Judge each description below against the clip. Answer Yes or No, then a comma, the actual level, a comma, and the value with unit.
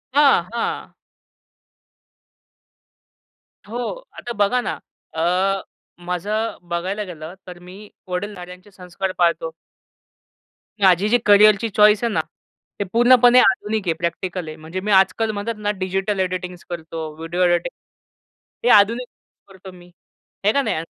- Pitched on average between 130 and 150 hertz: No, high, 190 Hz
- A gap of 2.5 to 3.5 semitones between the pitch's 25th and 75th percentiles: Yes, average, 3.1 semitones